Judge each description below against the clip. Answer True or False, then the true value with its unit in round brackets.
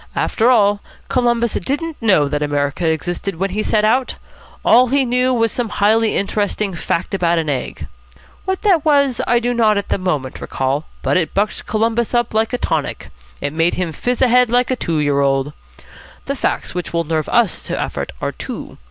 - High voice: True (210 Hz)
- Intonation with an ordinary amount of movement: False (6.6 semitones)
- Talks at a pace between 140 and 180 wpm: False (195 wpm)